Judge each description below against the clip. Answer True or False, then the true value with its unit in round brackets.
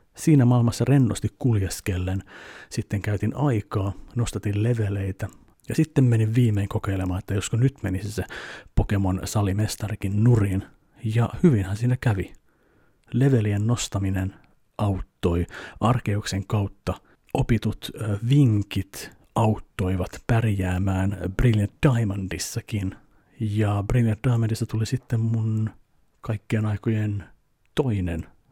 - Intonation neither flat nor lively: True (3.1 semitones)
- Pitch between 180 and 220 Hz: False (105 Hz)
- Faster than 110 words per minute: False (95 wpm)